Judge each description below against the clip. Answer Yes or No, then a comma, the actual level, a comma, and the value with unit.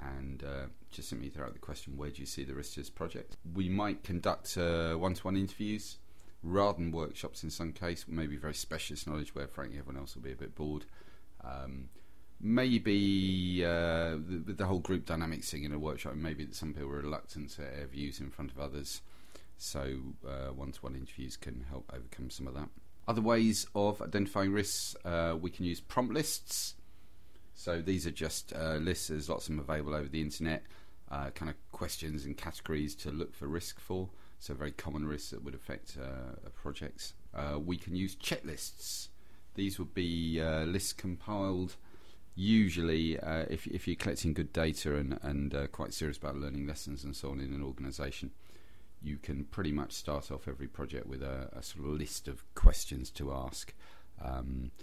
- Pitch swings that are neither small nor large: Yes, average, 4.0 semitones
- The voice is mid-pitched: No, very low, 80 Hz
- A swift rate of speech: No, average, 195 wpm